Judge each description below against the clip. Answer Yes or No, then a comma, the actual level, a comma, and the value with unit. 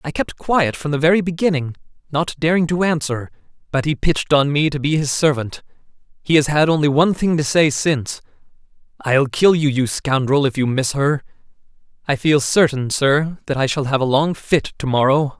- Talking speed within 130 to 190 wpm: No, average, 200 wpm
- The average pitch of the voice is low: No, medium, 145 Hz